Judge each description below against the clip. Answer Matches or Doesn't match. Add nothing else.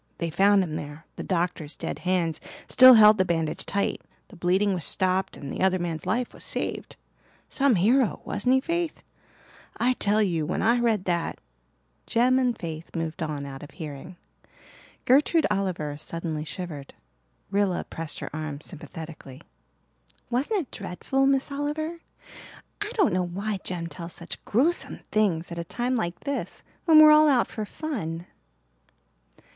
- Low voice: Doesn't match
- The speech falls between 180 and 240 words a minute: Doesn't match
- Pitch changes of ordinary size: Doesn't match